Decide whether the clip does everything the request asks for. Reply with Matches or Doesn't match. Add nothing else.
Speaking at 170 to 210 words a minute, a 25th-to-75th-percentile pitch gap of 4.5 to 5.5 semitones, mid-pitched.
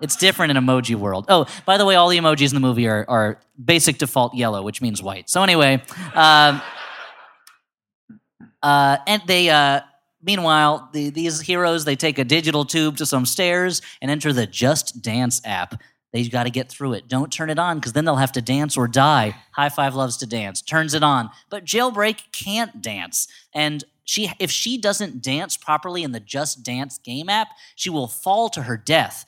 Matches